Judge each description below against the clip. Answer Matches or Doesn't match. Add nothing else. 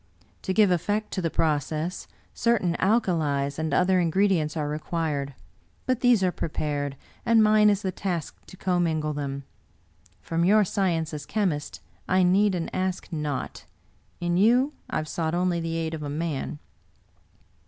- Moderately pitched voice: Matches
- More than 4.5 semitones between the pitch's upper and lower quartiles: Doesn't match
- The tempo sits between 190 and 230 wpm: Doesn't match